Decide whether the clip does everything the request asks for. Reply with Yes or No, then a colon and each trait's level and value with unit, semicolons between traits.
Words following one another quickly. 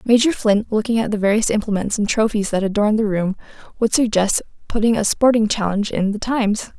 No: average, 195 wpm